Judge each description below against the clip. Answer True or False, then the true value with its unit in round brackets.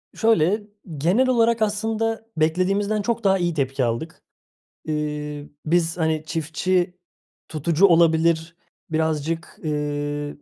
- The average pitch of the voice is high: False (165 Hz)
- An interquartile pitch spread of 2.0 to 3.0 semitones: False (4.6 semitones)